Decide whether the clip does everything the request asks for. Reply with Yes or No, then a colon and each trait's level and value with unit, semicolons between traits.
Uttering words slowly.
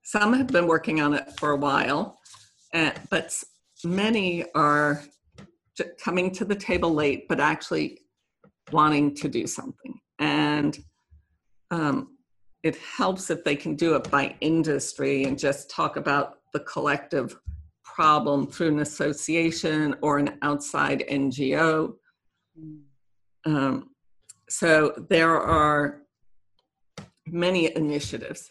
Yes: slow, 115 wpm